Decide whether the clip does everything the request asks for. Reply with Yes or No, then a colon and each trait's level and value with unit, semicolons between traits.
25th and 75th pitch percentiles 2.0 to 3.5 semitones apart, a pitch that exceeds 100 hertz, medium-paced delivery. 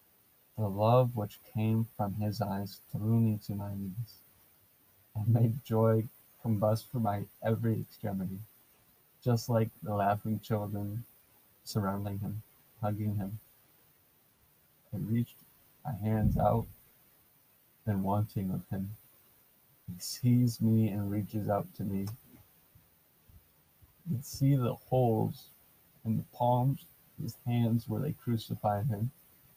No: average, 2.9 semitones; low, 110 Hz; slow, 125 wpm